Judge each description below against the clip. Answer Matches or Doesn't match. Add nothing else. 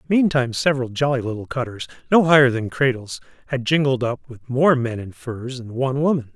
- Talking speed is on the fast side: Doesn't match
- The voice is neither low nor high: Doesn't match